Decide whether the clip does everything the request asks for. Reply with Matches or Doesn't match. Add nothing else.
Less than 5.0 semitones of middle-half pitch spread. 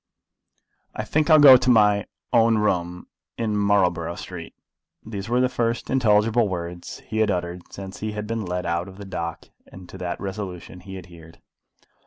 Matches